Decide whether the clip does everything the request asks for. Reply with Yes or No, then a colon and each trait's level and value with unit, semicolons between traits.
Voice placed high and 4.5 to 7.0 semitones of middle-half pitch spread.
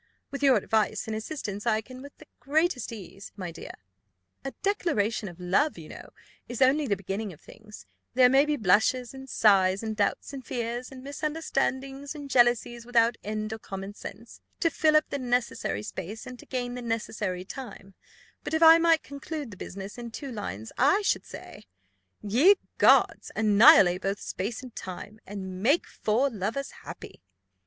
Yes: high, 235 Hz; average, 5.0 semitones